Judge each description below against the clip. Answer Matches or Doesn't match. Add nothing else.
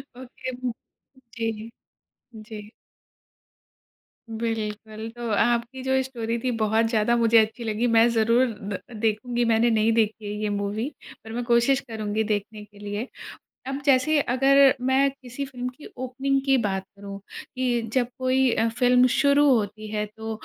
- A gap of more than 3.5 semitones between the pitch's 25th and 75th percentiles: Doesn't match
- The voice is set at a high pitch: Matches